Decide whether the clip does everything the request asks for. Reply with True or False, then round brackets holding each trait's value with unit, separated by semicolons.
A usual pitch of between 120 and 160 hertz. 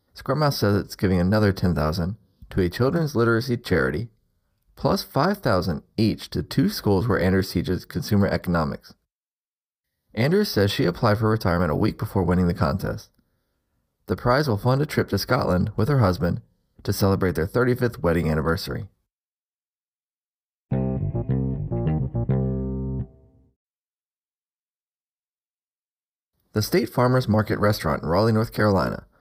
False (100 Hz)